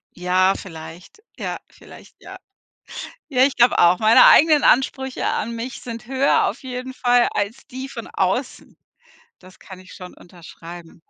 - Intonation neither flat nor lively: No, wide, 6.1 semitones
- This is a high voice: Yes, high, 230 Hz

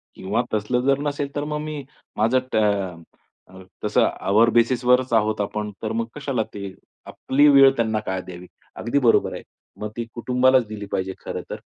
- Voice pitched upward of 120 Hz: No, low, 115 Hz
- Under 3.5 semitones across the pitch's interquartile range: No, average, 4.0 semitones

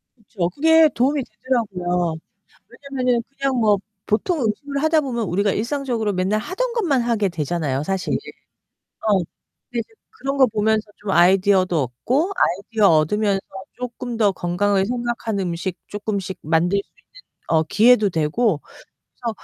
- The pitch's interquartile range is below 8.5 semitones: Yes, average, 5.2 semitones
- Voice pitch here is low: No, high, 215 Hz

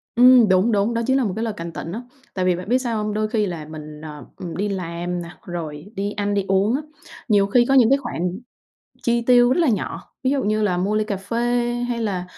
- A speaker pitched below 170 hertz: No, high, 205 Hz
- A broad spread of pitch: No, average, 4.7 semitones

